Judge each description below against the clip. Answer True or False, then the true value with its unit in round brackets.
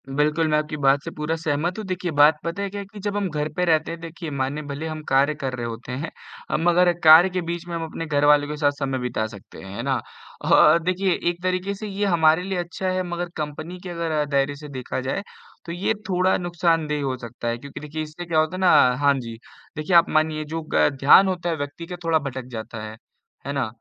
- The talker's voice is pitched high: False (155 Hz)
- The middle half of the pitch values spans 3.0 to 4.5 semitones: True (3.6 semitones)